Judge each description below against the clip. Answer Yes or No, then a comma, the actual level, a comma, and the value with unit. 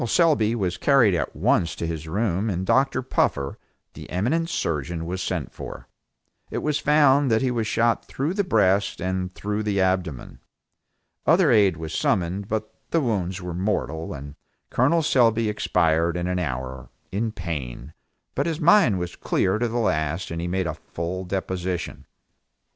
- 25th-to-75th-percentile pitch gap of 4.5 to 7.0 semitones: Yes, wide, 5.5 semitones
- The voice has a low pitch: Yes, very low, 95 Hz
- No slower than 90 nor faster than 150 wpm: No, average, 165 wpm